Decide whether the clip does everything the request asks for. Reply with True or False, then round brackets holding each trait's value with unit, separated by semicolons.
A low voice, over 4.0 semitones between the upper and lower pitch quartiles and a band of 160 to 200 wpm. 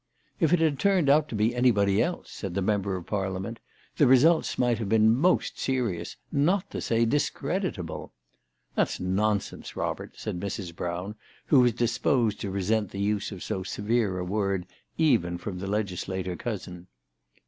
True (105 Hz; 5.1 semitones; 175 wpm)